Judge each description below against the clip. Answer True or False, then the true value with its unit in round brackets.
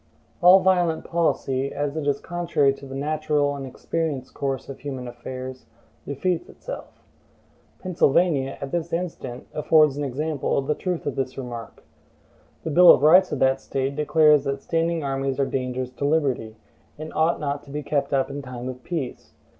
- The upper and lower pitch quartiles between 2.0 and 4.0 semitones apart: True (3.1 semitones)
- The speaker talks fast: False (175 wpm)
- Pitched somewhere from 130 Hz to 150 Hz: True (140 Hz)